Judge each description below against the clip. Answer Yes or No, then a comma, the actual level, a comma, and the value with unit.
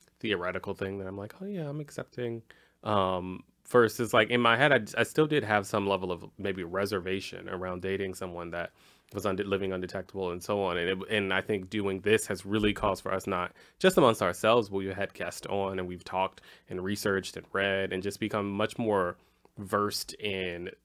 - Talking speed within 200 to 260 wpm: Yes, fast, 205 wpm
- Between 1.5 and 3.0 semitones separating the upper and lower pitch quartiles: Yes, narrow, 2.4 semitones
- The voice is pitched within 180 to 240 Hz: No, low, 100 Hz